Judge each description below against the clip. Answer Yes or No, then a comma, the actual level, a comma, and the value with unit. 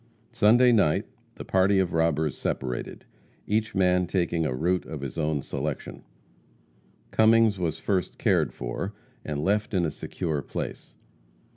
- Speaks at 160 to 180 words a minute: No, average, 140 wpm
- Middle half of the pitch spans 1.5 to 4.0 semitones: No, average, 4.8 semitones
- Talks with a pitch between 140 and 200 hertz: No, very low, 85 Hz